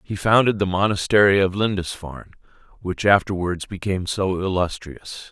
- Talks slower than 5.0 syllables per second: No, 5.1 syllables/s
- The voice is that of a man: Yes, male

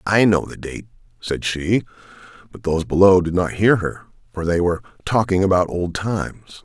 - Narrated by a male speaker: Yes, male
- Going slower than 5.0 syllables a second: No, 5.5 syllables/s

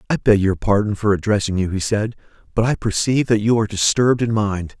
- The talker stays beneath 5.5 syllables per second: No, 6.2 syllables/s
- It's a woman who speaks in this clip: No, male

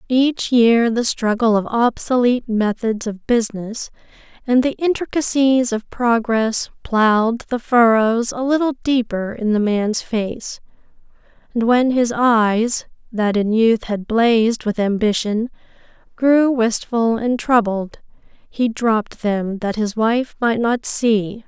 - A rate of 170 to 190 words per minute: No, slow, 135 wpm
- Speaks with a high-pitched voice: Yes, high, 230 Hz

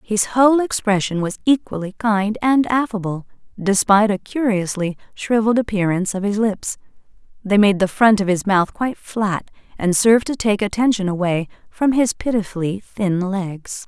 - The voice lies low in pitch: No, high, 205 Hz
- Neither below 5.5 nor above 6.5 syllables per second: No, 5.0 syllables/s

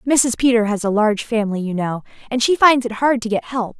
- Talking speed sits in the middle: No, fast, 255 wpm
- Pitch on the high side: Yes, high, 230 Hz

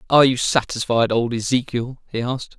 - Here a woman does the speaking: No, male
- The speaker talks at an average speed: Yes, average, 165 wpm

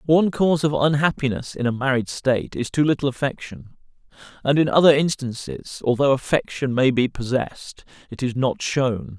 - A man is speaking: Yes, male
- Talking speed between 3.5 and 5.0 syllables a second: No, 5.3 syllables/s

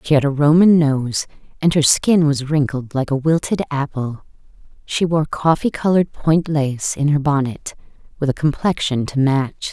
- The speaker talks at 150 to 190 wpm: Yes, average, 175 wpm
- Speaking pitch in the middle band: Yes, medium, 145 Hz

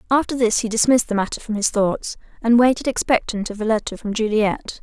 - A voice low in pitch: No, high, 225 Hz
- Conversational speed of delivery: No, fast, 210 wpm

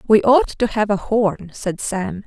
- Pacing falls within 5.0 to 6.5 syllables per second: No, 3.8 syllables/s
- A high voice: Yes, high, 210 Hz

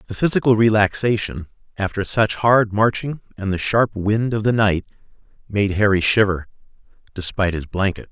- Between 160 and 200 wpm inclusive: No, average, 150 wpm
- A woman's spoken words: No, male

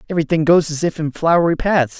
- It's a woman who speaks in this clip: No, male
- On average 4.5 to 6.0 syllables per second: No, 6.5 syllables/s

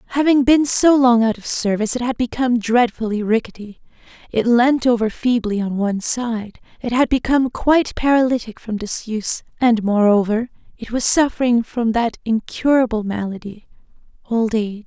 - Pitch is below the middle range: No, high, 235 Hz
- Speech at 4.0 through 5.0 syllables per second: No, 5.2 syllables/s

